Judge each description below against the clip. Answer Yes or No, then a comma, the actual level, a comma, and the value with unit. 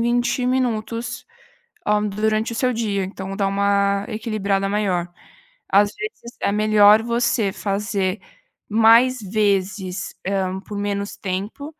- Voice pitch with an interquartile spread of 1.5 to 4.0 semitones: Yes, narrow, 2.6 semitones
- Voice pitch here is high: Yes, high, 210 Hz